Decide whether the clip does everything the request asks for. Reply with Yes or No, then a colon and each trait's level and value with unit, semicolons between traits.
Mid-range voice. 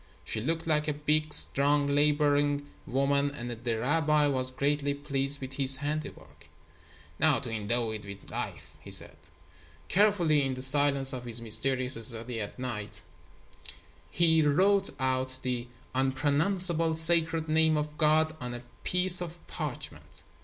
Yes: medium, 145 Hz